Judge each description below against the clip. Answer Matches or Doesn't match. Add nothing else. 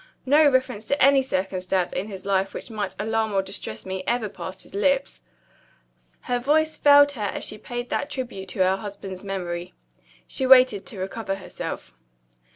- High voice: Matches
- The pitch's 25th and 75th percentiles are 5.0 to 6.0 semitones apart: Matches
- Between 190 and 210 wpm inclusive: Doesn't match